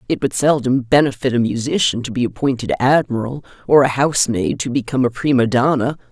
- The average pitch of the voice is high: No, low, 130 Hz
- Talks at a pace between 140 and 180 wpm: Yes, average, 175 wpm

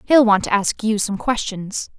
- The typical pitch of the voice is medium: No, high, 215 Hz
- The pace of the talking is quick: Yes, fast, 210 wpm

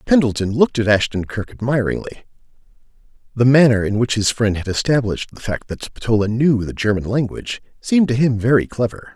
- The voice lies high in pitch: No, low, 115 Hz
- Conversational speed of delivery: Yes, average, 175 wpm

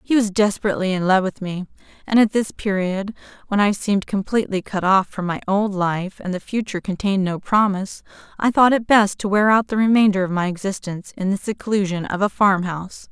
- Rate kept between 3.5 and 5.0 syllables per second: No, 5.8 syllables/s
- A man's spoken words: No, female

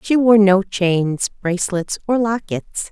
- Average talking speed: Yes, average, 145 wpm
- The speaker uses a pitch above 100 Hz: Yes, high, 200 Hz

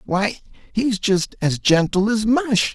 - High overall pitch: Yes, high, 210 Hz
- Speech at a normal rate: Yes, average, 155 wpm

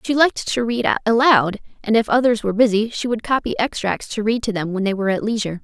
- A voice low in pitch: No, high, 220 Hz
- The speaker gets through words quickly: Yes, fast, 245 wpm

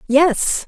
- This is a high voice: Yes, very high, 285 Hz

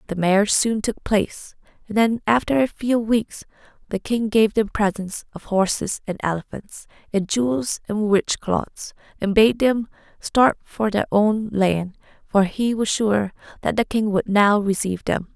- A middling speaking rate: Yes, average, 170 wpm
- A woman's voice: Yes, female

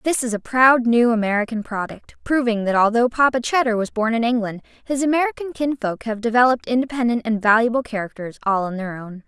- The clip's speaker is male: No, female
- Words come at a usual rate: Yes, average, 190 wpm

